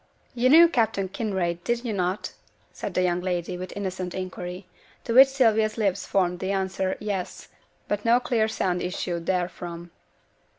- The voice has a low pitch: No, high, 190 Hz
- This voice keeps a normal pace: Yes, average, 160 wpm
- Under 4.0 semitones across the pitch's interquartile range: Yes, average, 3.6 semitones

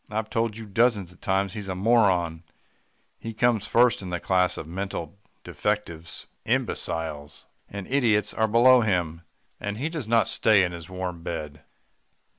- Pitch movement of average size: Yes, average, 4.2 semitones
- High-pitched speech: No, low, 100 Hz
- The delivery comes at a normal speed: Yes, average, 160 wpm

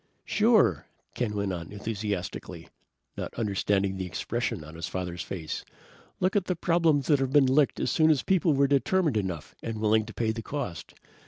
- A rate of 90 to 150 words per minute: No, average, 180 wpm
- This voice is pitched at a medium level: No, low, 115 Hz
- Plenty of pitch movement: Yes, wide, 7.2 semitones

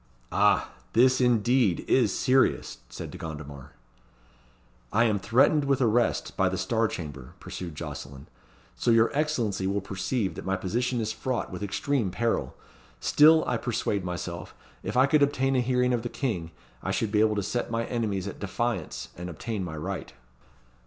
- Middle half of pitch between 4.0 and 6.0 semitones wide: Yes, average, 5.1 semitones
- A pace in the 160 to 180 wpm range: Yes, average, 170 wpm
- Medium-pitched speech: No, low, 110 Hz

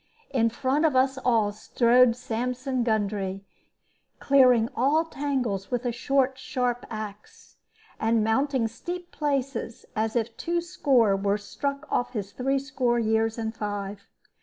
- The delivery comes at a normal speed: No, slow, 130 wpm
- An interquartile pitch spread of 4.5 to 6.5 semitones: No, average, 3.5 semitones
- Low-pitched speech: No, high, 245 Hz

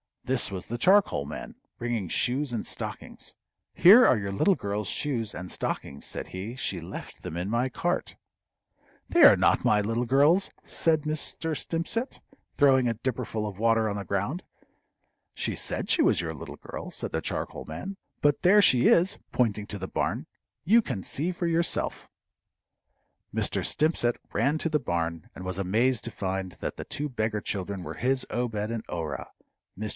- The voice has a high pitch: No, low, 115 Hz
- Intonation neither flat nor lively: No, wide, 6.9 semitones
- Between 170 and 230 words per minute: Yes, average, 175 wpm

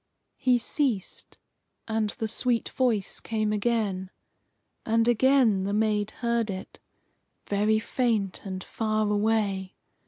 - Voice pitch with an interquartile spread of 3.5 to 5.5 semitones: No, narrow, 2.4 semitones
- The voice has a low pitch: No, high, 220 Hz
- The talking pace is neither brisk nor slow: No, slow, 115 wpm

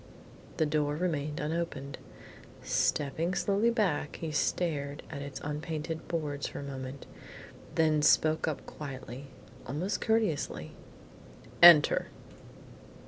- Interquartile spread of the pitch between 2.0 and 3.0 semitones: Yes, average, 2.7 semitones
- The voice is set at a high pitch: No, medium, 150 Hz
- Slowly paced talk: Yes, slow, 110 wpm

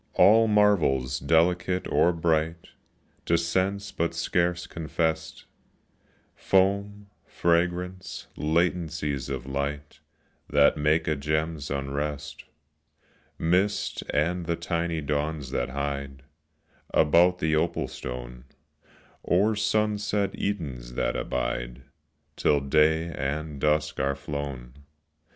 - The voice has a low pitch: Yes, very low, 80 Hz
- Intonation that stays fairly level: No, average, 3.8 semitones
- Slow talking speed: Yes, slow, 100 wpm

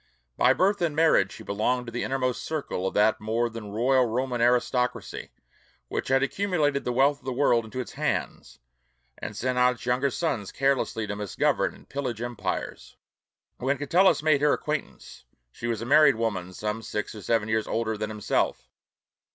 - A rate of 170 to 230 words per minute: Yes, average, 180 wpm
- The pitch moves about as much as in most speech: Yes, average, 3.9 semitones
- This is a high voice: No, low, 125 Hz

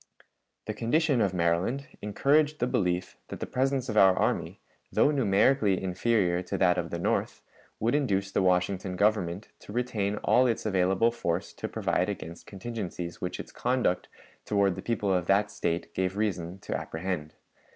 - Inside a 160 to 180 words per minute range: Yes, average, 165 wpm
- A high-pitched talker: No, low, 100 Hz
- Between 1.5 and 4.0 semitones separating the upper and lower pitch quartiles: No, average, 4.5 semitones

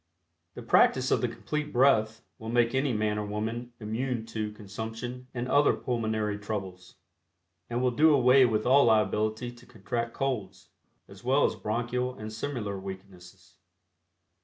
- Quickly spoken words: No, average, 150 wpm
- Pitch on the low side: Yes, low, 115 Hz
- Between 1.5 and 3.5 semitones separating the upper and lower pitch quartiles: Yes, average, 2.9 semitones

